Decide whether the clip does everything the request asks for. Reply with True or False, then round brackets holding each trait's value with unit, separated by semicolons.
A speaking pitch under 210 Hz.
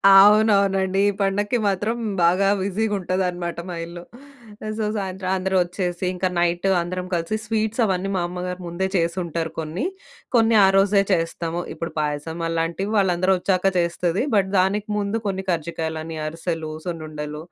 True (185 Hz)